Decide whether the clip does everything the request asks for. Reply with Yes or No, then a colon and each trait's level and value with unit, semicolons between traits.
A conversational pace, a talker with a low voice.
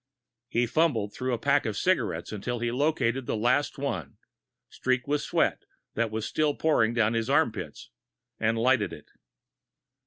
Yes: average, 160 wpm; low, 120 Hz